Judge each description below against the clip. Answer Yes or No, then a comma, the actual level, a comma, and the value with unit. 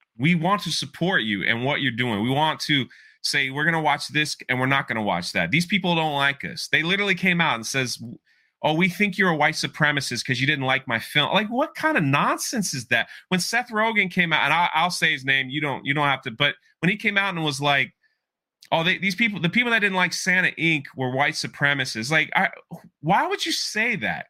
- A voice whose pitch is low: No, medium, 155 Hz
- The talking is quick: Yes, fast, 250 wpm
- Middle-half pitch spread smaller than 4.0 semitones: No, average, 5.3 semitones